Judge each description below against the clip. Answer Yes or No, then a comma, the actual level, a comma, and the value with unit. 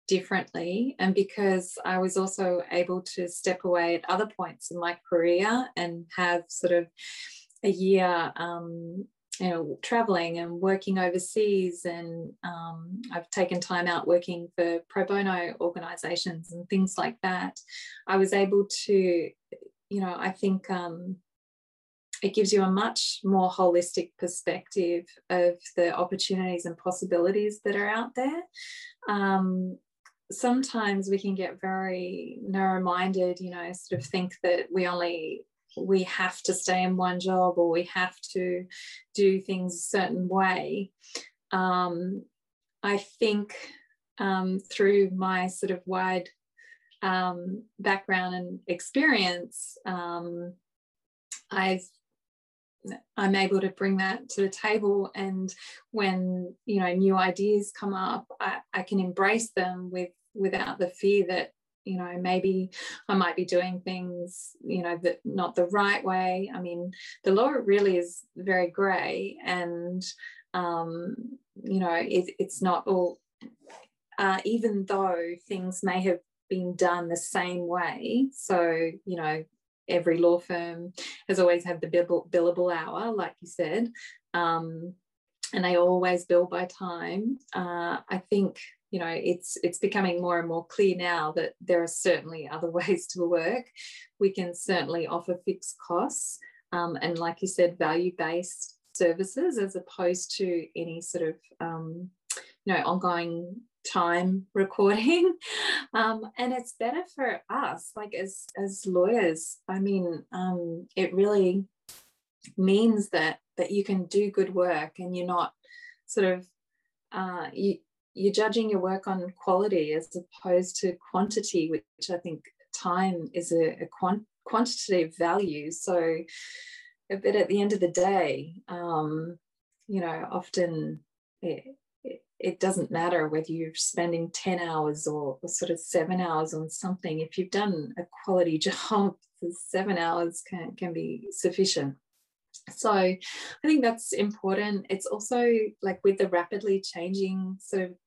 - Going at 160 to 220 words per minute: No, average, 145 wpm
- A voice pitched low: No, medium, 185 Hz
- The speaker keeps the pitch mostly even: Yes, narrow, 2.2 semitones